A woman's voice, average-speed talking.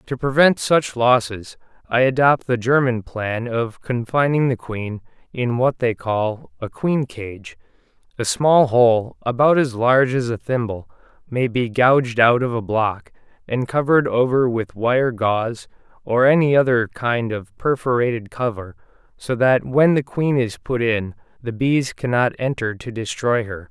No: male; average, 160 wpm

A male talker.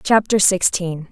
No: female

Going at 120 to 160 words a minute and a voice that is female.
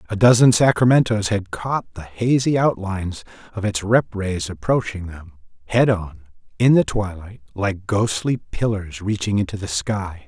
No: average, 150 wpm; male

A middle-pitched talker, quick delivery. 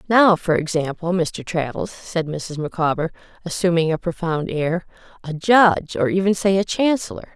No: medium, 175 Hz; average, 155 wpm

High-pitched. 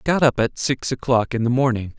No: low, 125 Hz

